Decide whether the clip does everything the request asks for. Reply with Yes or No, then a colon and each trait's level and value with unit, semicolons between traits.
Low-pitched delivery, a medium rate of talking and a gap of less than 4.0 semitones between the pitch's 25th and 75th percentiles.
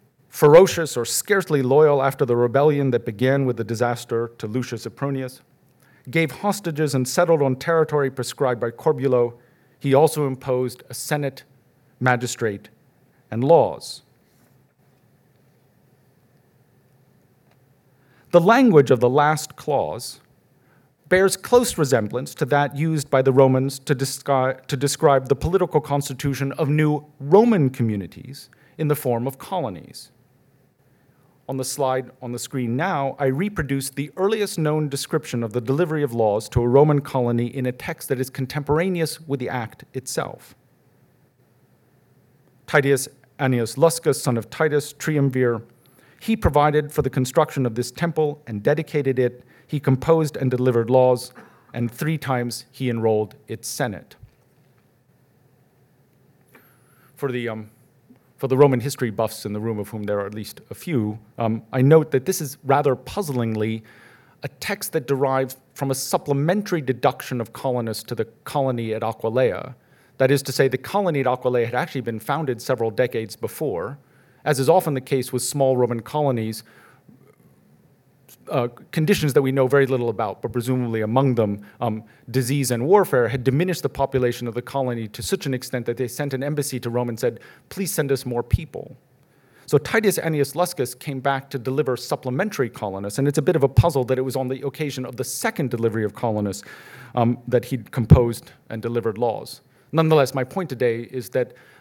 Yes: low, 130 Hz; average, 160 wpm; average, 3.1 semitones